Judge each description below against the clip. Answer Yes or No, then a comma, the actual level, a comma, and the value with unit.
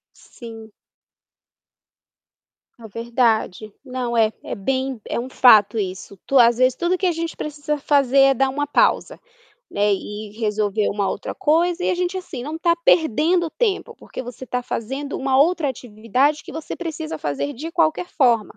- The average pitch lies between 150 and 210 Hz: No, very high, 260 Hz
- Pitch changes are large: Yes, wide, 5.9 semitones